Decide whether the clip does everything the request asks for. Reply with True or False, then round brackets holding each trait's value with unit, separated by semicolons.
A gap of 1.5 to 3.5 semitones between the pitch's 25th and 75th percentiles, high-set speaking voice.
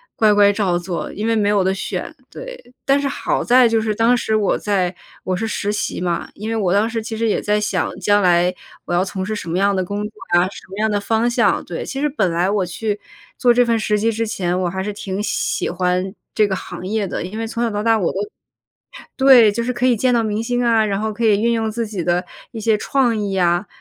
True (3.1 semitones; 210 Hz)